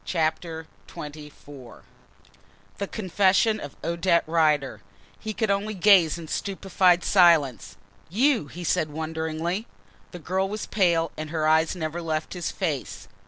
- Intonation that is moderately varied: Yes, average, 3.4 semitones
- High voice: No, medium, 170 Hz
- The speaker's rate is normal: No, slow, 130 wpm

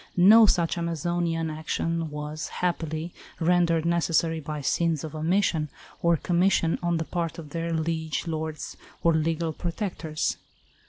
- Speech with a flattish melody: Yes, narrow, 1.5 semitones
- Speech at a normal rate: No, slow, 130 wpm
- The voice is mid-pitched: Yes, medium, 165 Hz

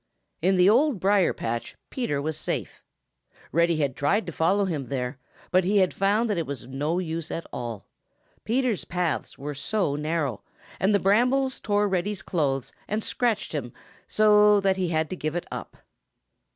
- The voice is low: No, medium, 180 Hz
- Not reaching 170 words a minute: No, average, 180 wpm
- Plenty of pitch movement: Yes, wide, 5.7 semitones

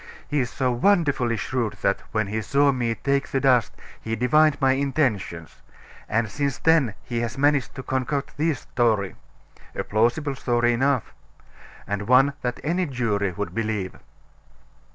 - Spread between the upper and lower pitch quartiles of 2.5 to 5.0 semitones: Yes, average, 3.9 semitones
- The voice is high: No, low, 125 Hz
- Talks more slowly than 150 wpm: No, average, 155 wpm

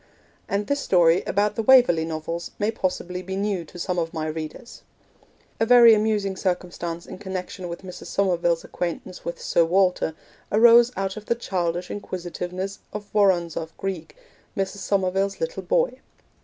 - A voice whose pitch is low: No, high, 190 Hz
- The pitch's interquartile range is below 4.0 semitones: Yes, average, 3.1 semitones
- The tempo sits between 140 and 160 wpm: Yes, average, 155 wpm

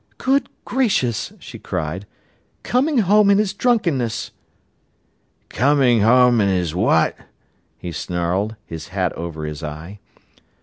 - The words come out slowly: Yes, slow, 120 wpm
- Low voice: Yes, low, 110 Hz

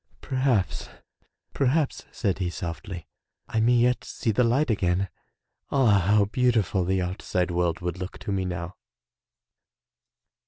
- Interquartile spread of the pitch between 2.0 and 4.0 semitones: No, average, 5.3 semitones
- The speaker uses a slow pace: Yes, slow, 130 wpm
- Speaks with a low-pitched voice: Yes, low, 100 Hz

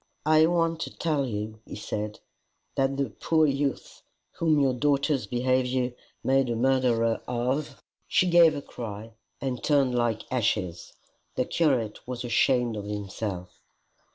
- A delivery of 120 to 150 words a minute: Yes, average, 145 wpm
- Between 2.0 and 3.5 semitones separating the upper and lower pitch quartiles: No, average, 4.0 semitones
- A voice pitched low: Yes, low, 125 Hz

